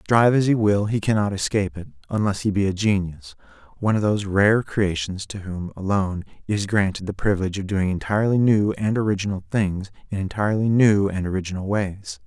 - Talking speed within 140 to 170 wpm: No, average, 180 wpm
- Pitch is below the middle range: Yes, low, 100 Hz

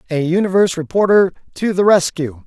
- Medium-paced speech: Yes, average, 145 wpm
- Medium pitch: Yes, medium, 175 Hz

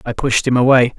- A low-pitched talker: Yes, low, 125 Hz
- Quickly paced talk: Yes, fast, 245 wpm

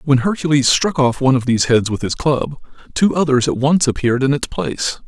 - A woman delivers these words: No, male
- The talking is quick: Yes, fast, 225 wpm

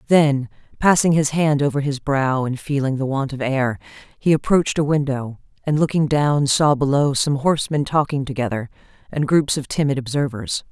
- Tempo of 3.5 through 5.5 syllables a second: Yes, 5.1 syllables/s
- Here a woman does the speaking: Yes, female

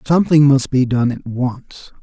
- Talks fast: No, average, 175 wpm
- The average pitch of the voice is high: No, low, 135 Hz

